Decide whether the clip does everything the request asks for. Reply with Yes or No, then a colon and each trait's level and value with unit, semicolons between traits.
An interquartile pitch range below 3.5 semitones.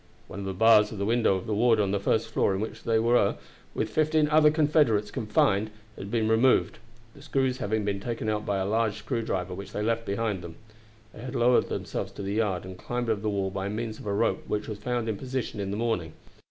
Yes: average, 2.8 semitones